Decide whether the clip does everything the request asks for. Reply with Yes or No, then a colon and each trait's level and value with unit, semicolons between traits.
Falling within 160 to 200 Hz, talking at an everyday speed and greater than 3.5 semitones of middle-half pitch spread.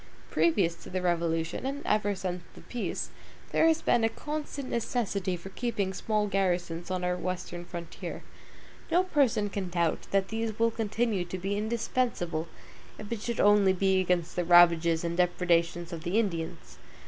Yes: high, 190 Hz; average, 165 wpm; average, 4.3 semitones